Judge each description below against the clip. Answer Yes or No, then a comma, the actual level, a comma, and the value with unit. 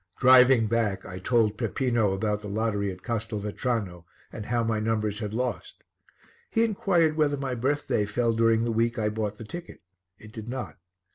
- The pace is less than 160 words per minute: No, average, 170 wpm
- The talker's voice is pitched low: Yes, low, 115 Hz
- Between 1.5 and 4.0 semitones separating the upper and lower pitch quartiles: Yes, average, 3.1 semitones